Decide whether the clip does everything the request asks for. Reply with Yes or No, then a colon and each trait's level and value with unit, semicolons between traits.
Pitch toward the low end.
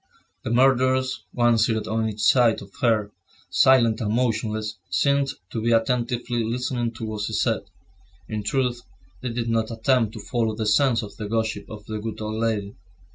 Yes: low, 115 Hz